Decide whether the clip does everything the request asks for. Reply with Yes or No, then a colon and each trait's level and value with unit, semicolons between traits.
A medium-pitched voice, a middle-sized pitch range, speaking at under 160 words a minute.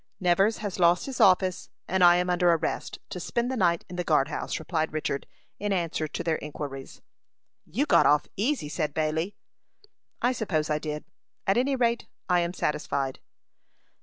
No: medium, 175 Hz; average, 4.1 semitones; average, 175 wpm